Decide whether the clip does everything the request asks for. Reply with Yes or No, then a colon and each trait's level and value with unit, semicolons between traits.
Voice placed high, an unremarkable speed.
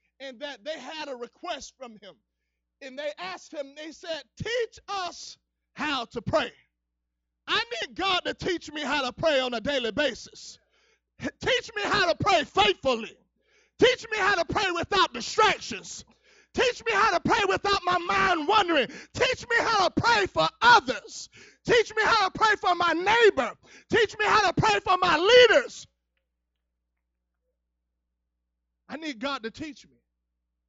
Yes: very high, 320 Hz; average, 160 wpm